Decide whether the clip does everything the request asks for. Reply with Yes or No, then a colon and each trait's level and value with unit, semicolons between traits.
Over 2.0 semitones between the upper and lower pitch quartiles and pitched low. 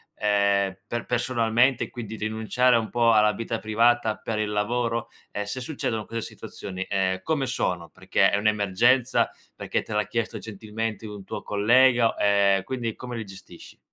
Yes: average, 2.7 semitones; low, 110 Hz